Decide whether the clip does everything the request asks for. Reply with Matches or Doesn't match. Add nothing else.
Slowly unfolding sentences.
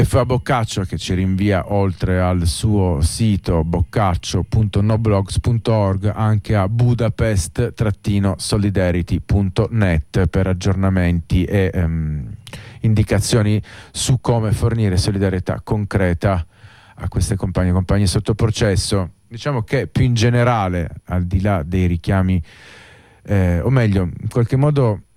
Matches